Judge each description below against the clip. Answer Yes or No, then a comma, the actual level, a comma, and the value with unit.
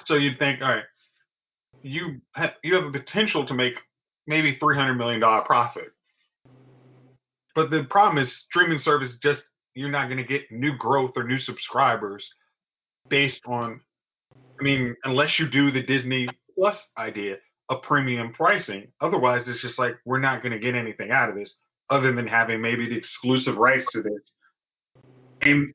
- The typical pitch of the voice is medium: No, low, 130 Hz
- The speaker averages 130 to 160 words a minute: No, average, 170 wpm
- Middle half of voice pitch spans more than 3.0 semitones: No, narrow, 2.6 semitones